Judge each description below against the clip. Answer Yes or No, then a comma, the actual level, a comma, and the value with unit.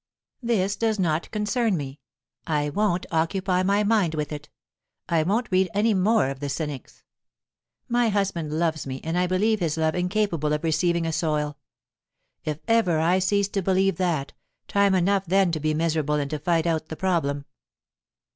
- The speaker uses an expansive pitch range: No, average, 4.3 semitones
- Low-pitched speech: No, medium, 175 Hz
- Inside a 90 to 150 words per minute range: No, average, 175 wpm